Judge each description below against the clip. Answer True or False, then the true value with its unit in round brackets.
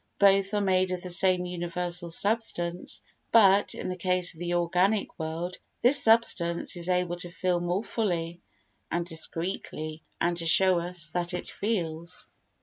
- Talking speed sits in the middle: True (155 wpm)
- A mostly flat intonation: True (1.8 semitones)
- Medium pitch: True (180 Hz)